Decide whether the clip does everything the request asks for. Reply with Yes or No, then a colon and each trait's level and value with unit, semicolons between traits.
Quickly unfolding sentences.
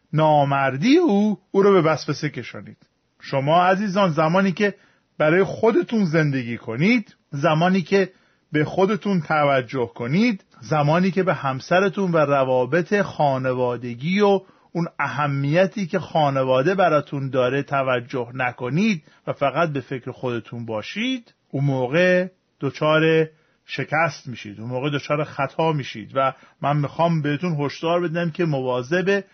No: average, 125 wpm